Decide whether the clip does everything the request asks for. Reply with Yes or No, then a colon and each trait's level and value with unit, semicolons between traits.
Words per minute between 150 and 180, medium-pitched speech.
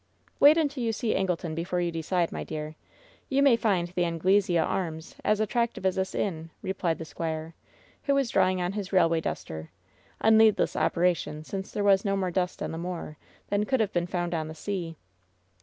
No: average, 200 wpm; medium, 180 Hz